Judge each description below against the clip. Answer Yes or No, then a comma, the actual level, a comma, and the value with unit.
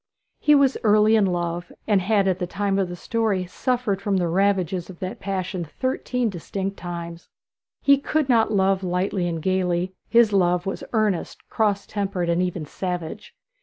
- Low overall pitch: No, high, 190 Hz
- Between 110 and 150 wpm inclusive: No, average, 170 wpm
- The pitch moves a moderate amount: Yes, average, 3.0 semitones